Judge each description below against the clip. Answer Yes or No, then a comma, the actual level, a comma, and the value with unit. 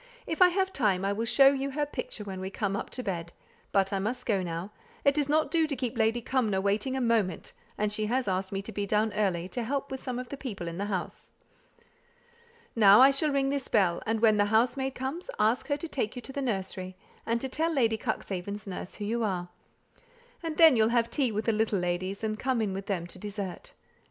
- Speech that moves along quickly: Yes, fast, 235 wpm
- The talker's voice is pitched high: Yes, high, 220 Hz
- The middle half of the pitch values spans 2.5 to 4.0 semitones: No, average, 5.1 semitones